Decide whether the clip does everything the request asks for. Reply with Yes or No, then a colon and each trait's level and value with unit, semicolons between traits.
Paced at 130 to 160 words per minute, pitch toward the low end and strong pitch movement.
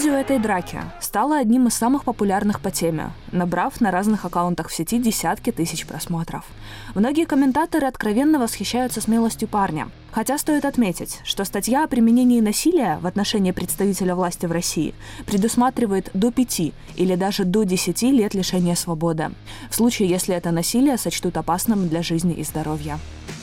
No: average, 155 wpm; high, 195 Hz; wide, 5.7 semitones